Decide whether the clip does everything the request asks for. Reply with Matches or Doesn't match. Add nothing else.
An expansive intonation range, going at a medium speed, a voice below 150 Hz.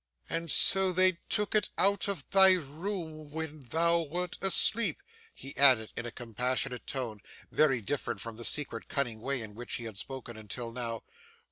Matches